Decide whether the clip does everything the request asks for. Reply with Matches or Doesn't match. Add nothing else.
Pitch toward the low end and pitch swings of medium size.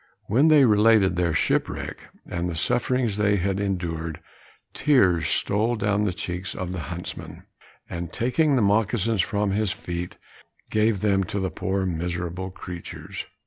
Matches